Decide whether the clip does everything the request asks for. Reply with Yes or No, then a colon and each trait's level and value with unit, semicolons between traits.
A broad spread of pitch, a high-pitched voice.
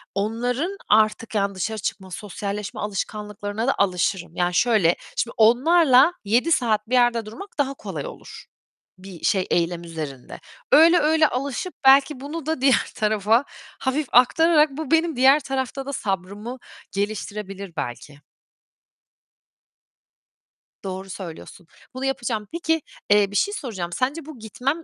Yes: wide, 5.7 semitones; high, 225 Hz